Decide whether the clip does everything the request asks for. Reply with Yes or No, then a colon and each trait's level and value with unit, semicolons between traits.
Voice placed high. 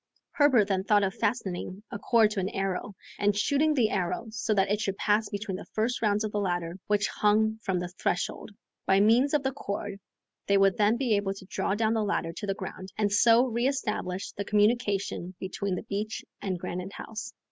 Yes: high, 205 Hz